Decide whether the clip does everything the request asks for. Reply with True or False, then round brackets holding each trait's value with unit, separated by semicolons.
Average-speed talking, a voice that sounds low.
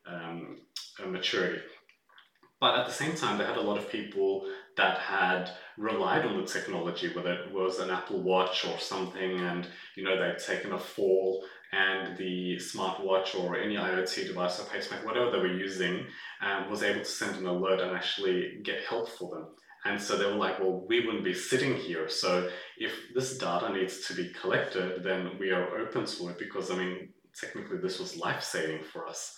True (195 wpm; 95 Hz)